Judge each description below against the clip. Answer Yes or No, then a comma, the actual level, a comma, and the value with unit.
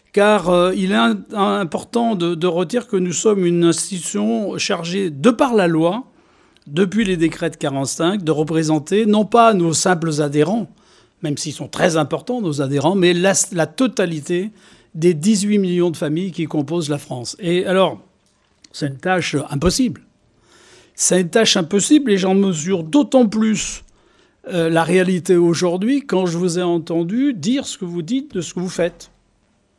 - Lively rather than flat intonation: No, average, 3.9 semitones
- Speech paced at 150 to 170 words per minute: Yes, average, 165 wpm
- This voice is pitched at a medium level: Yes, medium, 180 Hz